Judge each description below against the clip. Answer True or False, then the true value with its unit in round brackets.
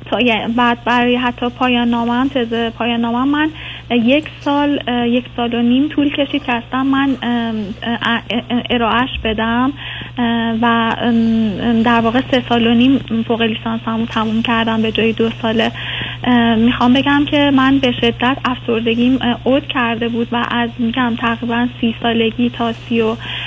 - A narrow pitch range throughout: True (1.4 semitones)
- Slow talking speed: False (140 wpm)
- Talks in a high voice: True (235 Hz)